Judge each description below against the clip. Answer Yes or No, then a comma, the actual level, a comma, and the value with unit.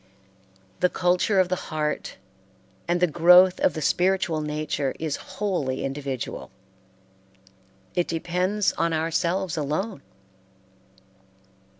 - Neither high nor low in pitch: Yes, medium, 170 Hz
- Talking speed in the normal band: No, slow, 100 wpm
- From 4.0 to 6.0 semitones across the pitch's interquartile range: No, average, 3.3 semitones